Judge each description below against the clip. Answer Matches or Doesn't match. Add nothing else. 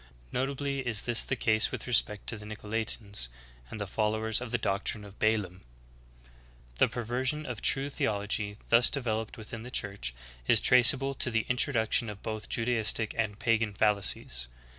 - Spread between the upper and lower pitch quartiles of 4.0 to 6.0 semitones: Doesn't match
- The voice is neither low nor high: Doesn't match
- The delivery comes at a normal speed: Matches